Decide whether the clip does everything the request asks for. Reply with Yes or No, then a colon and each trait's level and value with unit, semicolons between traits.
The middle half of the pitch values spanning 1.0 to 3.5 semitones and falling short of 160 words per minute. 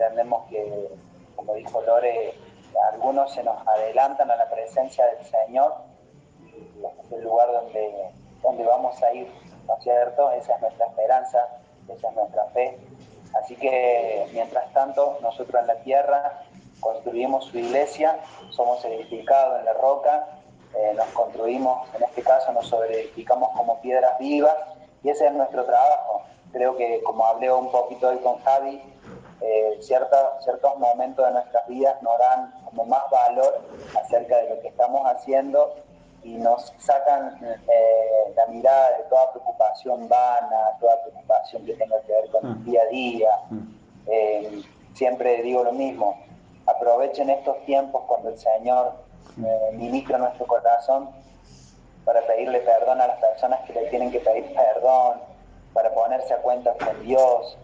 Yes: average, 3.0 semitones; average, 150 wpm